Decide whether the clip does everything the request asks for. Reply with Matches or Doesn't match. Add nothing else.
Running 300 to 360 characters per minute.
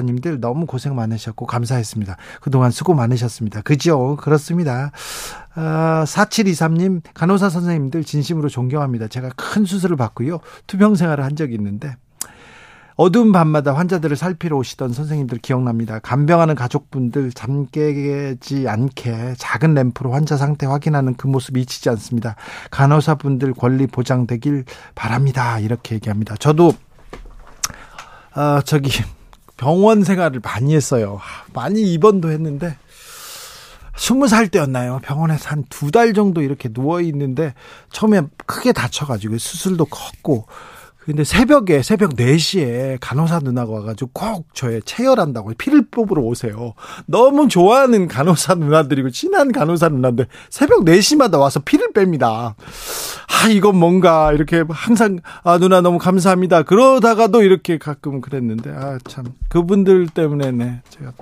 Matches